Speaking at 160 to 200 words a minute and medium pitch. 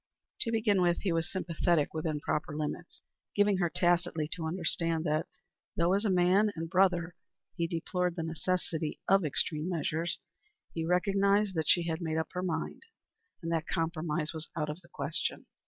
Yes: average, 170 wpm; medium, 170 Hz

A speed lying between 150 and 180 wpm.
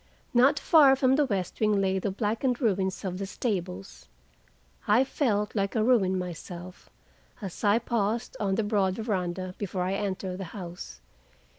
Yes: average, 160 wpm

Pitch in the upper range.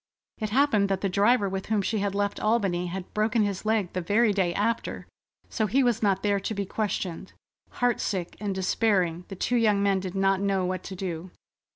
Yes: high, 200 Hz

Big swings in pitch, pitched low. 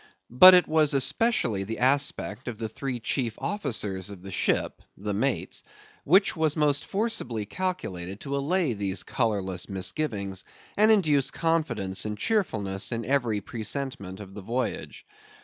Yes: wide, 7.3 semitones; low, 120 Hz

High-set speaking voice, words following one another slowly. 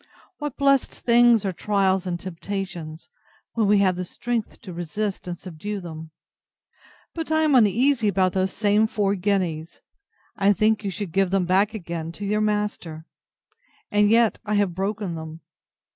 No: high, 200 Hz; average, 160 wpm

